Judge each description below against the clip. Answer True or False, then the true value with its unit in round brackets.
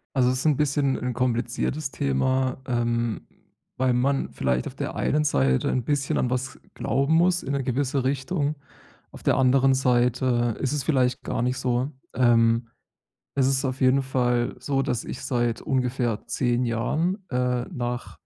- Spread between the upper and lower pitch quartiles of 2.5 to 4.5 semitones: False (2.1 semitones)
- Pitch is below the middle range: True (130 Hz)